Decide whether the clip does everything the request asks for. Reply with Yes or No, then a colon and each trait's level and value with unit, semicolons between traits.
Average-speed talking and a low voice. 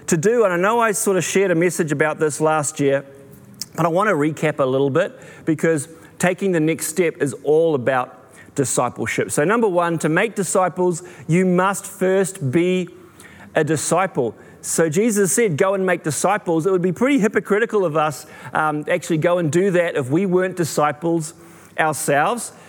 No: average, 185 wpm; medium, 170 Hz